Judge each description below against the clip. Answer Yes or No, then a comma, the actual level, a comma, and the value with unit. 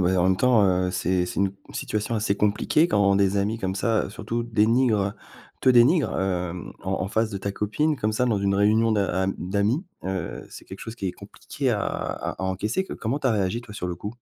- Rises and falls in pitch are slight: No, average, 3.1 semitones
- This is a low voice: Yes, low, 105 Hz